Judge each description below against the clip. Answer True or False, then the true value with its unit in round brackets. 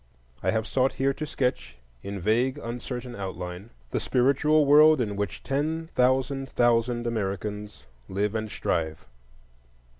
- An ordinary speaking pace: False (130 wpm)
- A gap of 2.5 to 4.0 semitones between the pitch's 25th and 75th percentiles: False (4.7 semitones)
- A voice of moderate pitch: False (120 Hz)